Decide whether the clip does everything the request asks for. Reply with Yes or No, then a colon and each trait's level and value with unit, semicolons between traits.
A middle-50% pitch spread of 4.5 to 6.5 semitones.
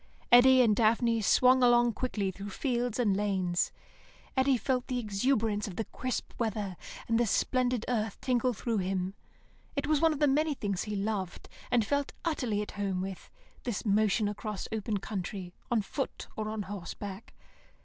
No: average, 3.8 semitones